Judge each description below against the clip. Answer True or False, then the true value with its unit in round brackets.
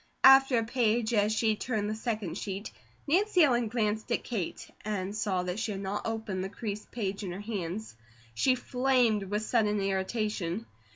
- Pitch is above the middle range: True (215 Hz)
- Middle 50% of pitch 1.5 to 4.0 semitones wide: True (2.9 semitones)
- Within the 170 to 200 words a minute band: True (175 wpm)